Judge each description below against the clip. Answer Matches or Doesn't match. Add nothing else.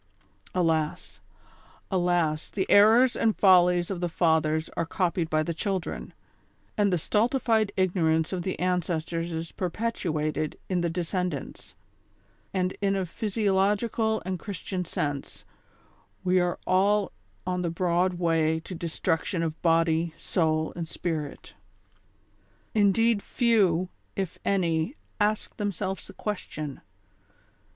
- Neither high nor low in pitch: Matches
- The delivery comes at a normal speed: Doesn't match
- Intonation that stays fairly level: Doesn't match